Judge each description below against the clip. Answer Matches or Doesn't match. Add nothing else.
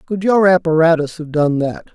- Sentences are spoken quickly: Doesn't match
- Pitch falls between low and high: Matches